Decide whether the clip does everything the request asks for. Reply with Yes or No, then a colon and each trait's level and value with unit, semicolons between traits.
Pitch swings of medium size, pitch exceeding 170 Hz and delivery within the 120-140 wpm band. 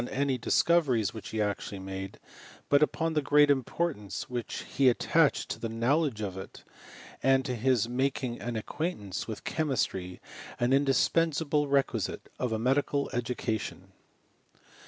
No: average, 4.4 semitones; low, 125 Hz; slow, 135 wpm